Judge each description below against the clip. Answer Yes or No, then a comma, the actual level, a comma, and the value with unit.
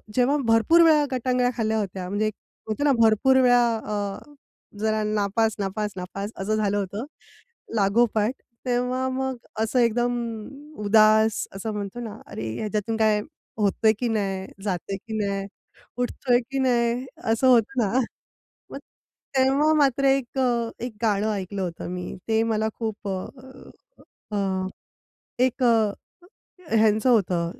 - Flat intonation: No, average, 3.2 semitones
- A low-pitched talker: No, high, 220 Hz